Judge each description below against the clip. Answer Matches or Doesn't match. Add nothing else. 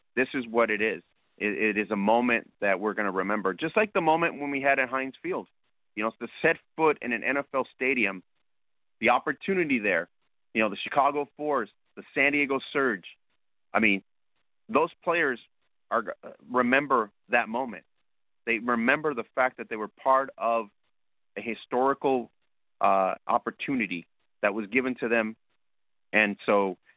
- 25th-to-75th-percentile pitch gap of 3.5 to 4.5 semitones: Matches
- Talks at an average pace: Matches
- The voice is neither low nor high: Doesn't match